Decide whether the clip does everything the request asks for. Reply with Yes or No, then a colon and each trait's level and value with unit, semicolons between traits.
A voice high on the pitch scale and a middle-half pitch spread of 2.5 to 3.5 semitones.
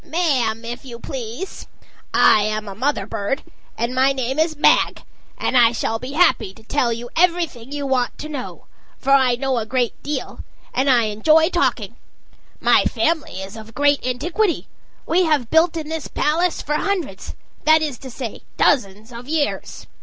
No: very high, 265 Hz; average, 5.0 semitones